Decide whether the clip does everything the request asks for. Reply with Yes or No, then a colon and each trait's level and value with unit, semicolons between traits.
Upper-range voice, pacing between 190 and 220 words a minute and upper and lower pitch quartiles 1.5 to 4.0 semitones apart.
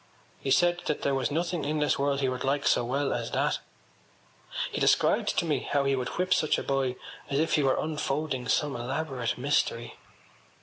No: medium, 140 Hz; average, 200 wpm; narrow, 2.6 semitones